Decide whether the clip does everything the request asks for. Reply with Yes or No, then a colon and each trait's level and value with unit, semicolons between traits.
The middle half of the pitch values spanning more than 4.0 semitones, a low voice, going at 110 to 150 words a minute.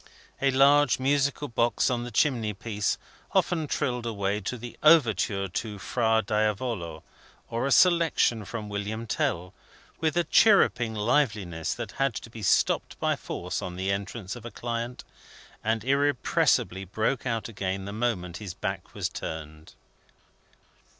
Yes: average, 4.4 semitones; low, 115 Hz; average, 145 wpm